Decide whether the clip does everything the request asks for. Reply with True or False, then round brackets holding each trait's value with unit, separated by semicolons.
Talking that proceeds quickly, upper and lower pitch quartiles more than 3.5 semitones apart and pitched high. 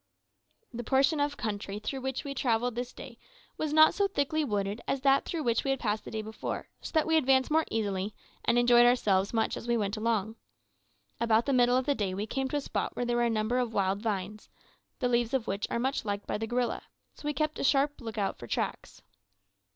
True (230 wpm; 4.0 semitones; 240 Hz)